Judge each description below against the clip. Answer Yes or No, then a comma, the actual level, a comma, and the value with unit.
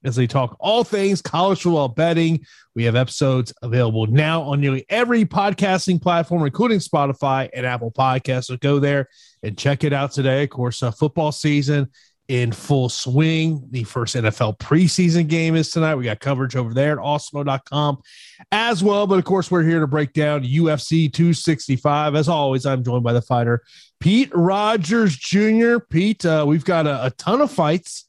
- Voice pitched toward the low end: No, medium, 145 Hz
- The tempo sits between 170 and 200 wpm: Yes, average, 180 wpm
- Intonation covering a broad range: No, average, 4.6 semitones